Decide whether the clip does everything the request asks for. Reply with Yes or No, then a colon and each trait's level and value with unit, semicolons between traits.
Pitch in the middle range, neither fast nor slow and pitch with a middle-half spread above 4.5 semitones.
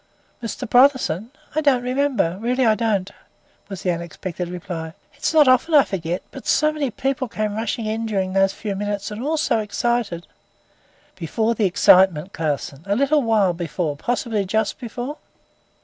No: high, 215 Hz; average, 165 wpm; average, 5.2 semitones